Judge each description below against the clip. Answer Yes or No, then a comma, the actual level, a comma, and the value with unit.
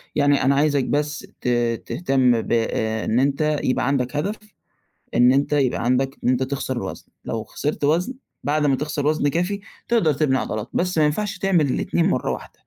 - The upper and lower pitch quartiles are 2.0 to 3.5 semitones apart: Yes, average, 3.0 semitones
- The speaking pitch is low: No, medium, 145 Hz